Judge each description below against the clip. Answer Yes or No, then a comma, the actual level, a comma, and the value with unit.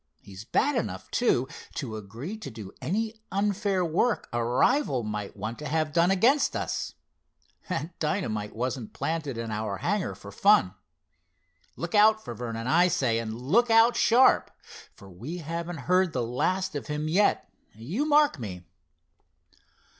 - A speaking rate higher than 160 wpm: No, average, 155 wpm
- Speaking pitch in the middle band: Yes, medium, 155 Hz